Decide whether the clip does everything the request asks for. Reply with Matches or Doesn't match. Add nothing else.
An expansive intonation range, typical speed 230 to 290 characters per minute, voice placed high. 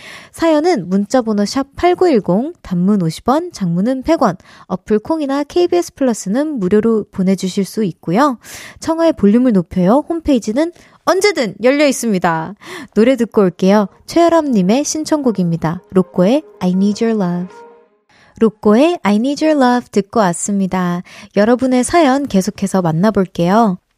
Doesn't match